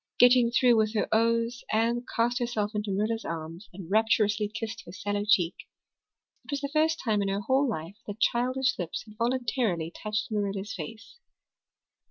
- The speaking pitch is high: Yes, high, 220 Hz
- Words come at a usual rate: Yes, average, 170 wpm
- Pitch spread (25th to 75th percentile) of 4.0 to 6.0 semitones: No, average, 2.8 semitones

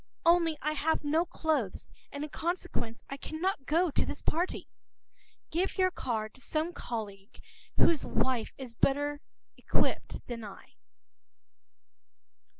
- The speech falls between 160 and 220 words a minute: No, slow, 135 wpm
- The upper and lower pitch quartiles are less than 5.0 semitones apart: No, wide, 5.5 semitones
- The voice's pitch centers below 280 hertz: No, very high, 290 Hz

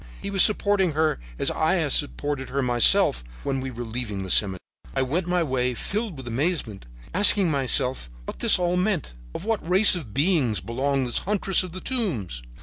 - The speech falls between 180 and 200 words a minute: Yes, average, 190 wpm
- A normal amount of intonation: No, wide, 7.2 semitones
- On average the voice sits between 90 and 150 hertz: Yes, medium, 140 Hz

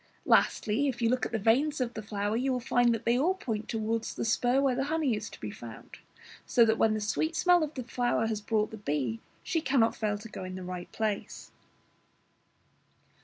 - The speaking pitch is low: No, high, 225 Hz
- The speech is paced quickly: Yes, fast, 225 wpm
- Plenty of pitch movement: No, average, 3.4 semitones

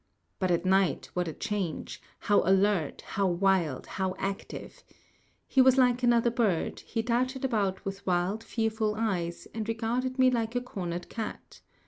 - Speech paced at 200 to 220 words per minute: No, average, 155 wpm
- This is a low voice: No, high, 210 Hz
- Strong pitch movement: No, average, 4.1 semitones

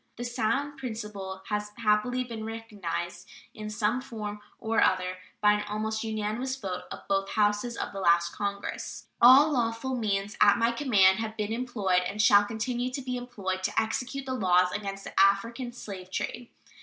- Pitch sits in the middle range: No, high, 215 Hz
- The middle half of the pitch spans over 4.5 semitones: No, average, 3.4 semitones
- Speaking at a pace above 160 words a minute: Yes, average, 170 wpm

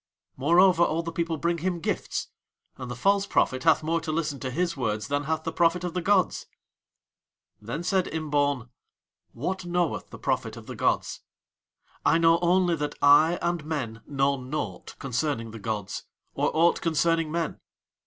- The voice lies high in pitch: No, medium, 160 Hz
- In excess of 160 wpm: Yes, average, 175 wpm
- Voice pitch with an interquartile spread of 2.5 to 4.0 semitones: Yes, average, 3.7 semitones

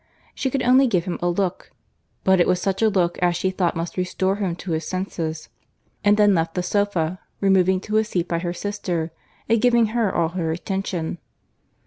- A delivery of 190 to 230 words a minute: Yes, average, 200 wpm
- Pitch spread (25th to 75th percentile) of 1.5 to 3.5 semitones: Yes, average, 2.9 semitones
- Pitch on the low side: No, medium, 185 Hz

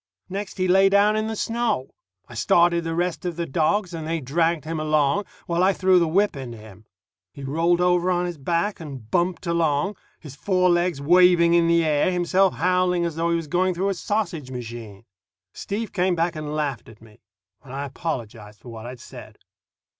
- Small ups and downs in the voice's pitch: No, average, 4.2 semitones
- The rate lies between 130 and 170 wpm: No, average, 200 wpm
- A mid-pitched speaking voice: Yes, medium, 170 Hz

